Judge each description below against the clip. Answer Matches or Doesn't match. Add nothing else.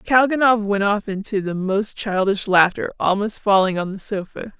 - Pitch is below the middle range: Doesn't match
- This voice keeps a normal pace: Matches